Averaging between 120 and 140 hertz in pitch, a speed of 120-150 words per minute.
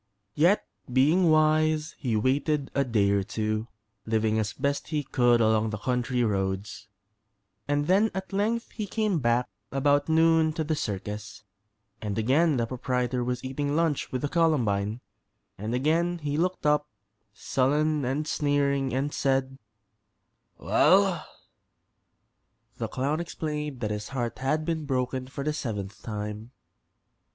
Yes: low, 135 Hz; average, 140 wpm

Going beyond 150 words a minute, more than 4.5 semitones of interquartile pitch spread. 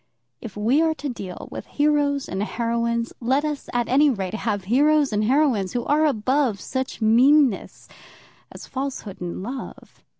Yes: average, 160 wpm; average, 5.0 semitones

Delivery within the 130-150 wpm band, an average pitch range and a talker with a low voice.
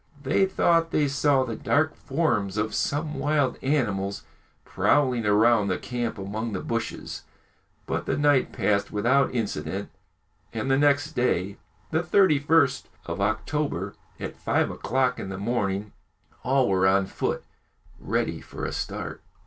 No: average, 140 wpm; wide, 5.9 semitones; low, 125 Hz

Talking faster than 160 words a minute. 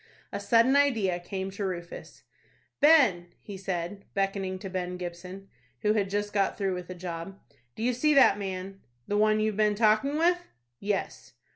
Yes: average, 170 wpm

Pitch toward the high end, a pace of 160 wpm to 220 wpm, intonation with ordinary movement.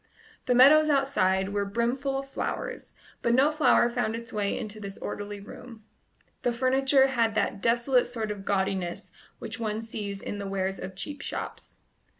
Yes: high, 230 Hz; average, 165 wpm; average, 4.5 semitones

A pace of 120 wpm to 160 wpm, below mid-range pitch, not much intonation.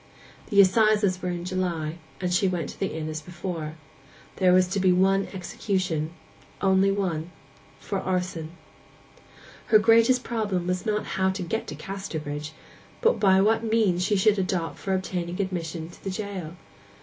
No: average, 150 wpm; medium, 185 Hz; narrow, 2.3 semitones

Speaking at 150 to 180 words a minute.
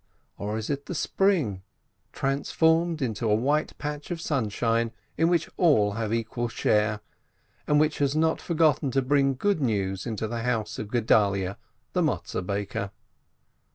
Yes: average, 155 wpm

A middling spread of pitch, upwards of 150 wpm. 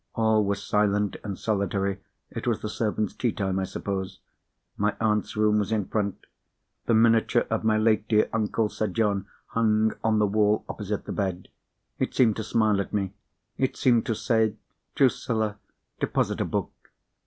No: narrow, 1.7 semitones; average, 165 wpm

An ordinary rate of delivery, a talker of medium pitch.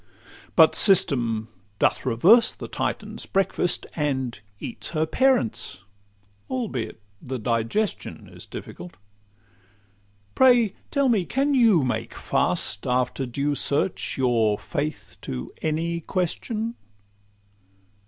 No: slow, 105 wpm; medium, 150 Hz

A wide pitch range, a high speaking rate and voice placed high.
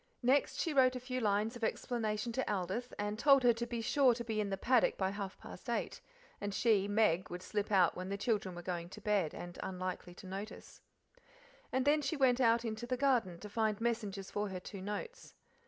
No: average, 3.8 semitones; fast, 220 wpm; high, 215 Hz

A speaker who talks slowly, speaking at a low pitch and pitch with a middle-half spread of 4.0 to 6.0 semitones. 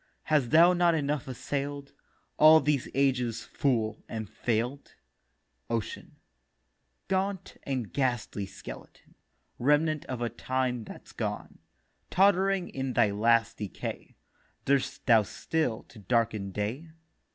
Yes: slow, 115 wpm; low, 130 Hz; average, 4.7 semitones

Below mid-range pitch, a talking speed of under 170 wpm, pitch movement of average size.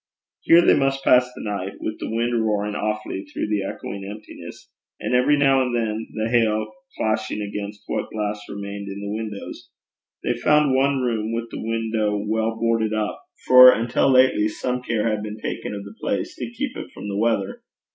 No: low, 110 Hz; average, 190 wpm; average, 3.0 semitones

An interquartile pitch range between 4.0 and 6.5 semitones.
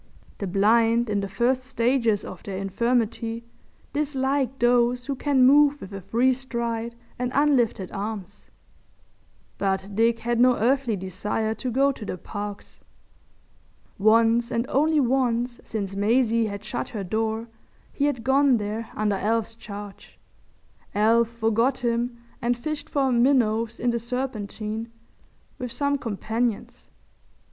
No: average, 2.9 semitones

